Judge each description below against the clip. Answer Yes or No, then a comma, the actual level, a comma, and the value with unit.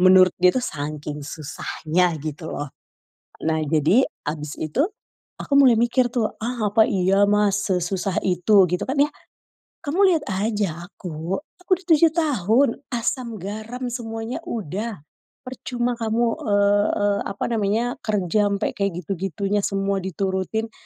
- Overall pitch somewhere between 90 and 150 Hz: No, high, 205 Hz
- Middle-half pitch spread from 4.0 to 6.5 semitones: Yes, average, 4.4 semitones